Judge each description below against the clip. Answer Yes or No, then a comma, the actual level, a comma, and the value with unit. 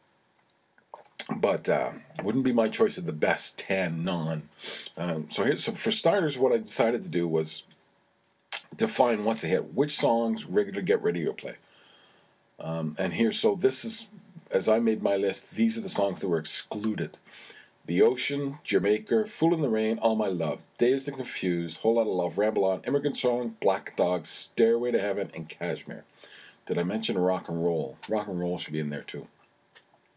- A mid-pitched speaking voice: No, low, 110 Hz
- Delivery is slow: No, average, 185 wpm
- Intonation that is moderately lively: No, wide, 6.9 semitones